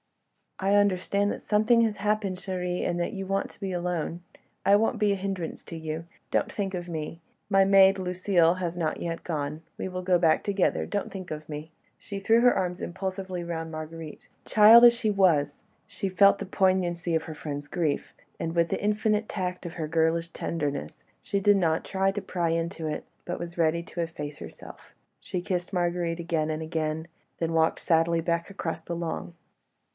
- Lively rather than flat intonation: No, average, 3.0 semitones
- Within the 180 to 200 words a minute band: Yes, average, 190 wpm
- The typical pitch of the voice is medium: Yes, medium, 175 Hz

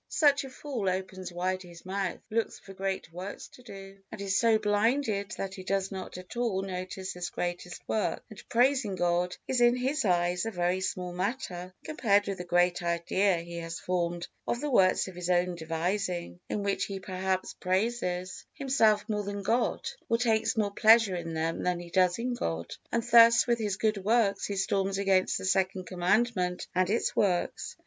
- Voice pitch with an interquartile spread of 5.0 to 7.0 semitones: No, average, 3.5 semitones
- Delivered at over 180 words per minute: Yes, average, 190 wpm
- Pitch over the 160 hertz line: Yes, high, 190 Hz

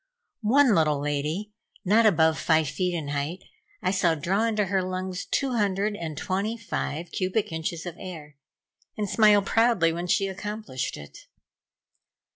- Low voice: No, medium, 185 Hz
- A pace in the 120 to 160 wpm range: Yes, average, 150 wpm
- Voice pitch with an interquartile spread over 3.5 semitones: Yes, average, 4.5 semitones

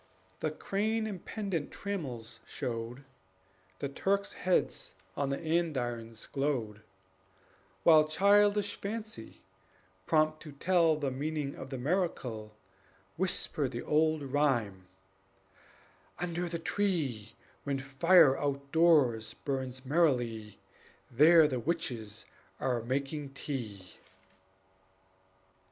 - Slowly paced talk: Yes, slow, 100 wpm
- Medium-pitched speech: Yes, medium, 145 Hz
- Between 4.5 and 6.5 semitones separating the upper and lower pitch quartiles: Yes, wide, 5.4 semitones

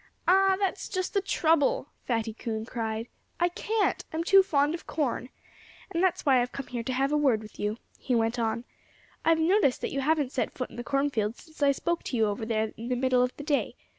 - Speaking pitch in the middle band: No, very high, 270 Hz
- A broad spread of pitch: Yes, wide, 5.7 semitones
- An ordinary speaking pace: No, fast, 225 wpm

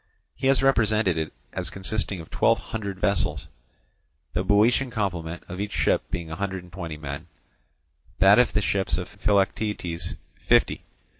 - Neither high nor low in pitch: No, very low, 95 Hz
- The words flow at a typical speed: Yes, average, 155 wpm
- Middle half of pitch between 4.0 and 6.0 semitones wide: No, average, 3.5 semitones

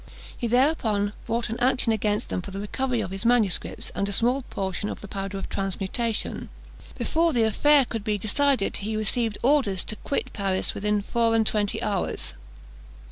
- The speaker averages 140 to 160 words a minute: No, average, 180 wpm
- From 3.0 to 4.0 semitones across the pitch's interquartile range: Yes, average, 3.3 semitones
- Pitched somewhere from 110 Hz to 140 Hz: No, high, 215 Hz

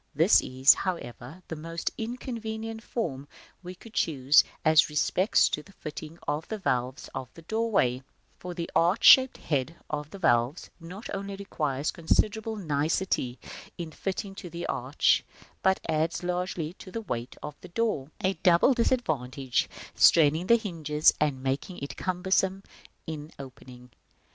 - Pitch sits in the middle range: Yes, medium, 165 Hz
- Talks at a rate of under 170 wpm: Yes, average, 145 wpm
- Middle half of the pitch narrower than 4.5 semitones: No, average, 5.2 semitones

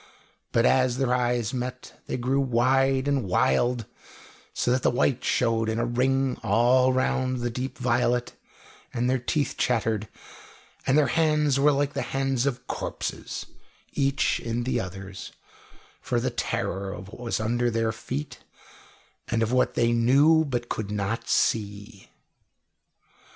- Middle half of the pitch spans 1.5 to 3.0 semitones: Yes, narrow, 2.6 semitones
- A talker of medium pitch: No, low, 125 Hz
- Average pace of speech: Yes, average, 145 wpm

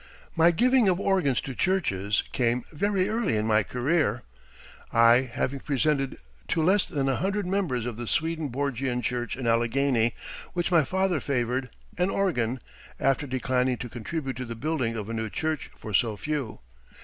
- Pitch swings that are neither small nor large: No, wide, 5.7 semitones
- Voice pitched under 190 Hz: Yes, low, 135 Hz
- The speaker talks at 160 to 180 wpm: Yes, average, 170 wpm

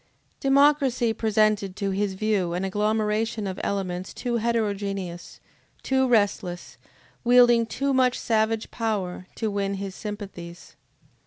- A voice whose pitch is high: Yes, high, 210 Hz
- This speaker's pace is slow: Yes, slow, 115 wpm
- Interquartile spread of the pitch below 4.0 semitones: Yes, average, 3.2 semitones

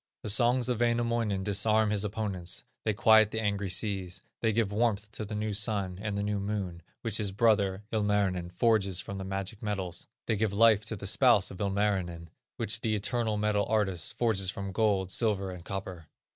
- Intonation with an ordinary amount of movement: No, narrow, 2.2 semitones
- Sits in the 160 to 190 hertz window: No, low, 105 Hz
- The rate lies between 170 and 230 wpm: Yes, average, 185 wpm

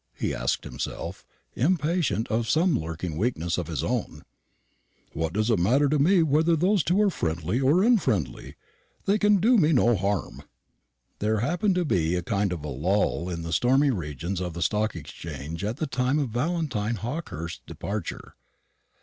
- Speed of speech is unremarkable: Yes, average, 165 wpm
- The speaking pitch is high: No, low, 110 Hz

